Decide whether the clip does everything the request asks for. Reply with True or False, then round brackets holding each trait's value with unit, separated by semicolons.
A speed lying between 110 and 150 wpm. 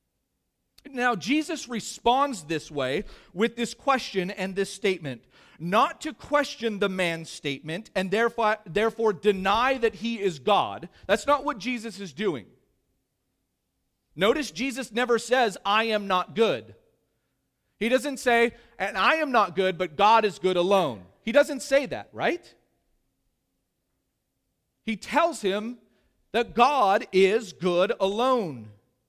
True (135 wpm)